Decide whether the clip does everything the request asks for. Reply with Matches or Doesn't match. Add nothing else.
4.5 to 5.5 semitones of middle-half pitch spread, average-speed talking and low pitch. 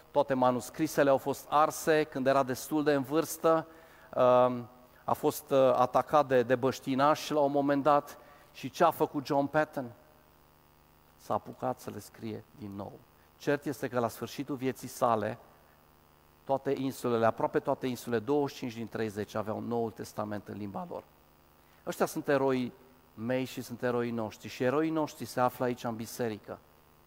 Matches